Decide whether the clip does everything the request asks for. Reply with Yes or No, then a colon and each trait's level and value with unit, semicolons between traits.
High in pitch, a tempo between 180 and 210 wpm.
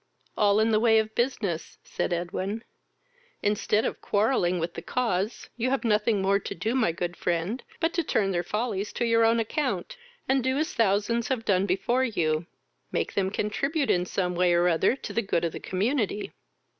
Yes: high, 210 Hz; average, 195 wpm